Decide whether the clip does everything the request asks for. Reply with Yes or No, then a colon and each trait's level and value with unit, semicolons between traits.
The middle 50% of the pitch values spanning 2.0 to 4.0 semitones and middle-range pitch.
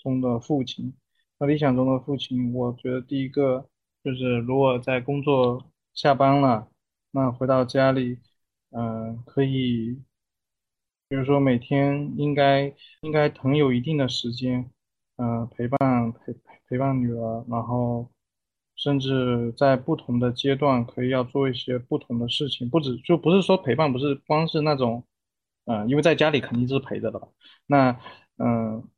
No: narrow, 2.5 semitones; low, 130 Hz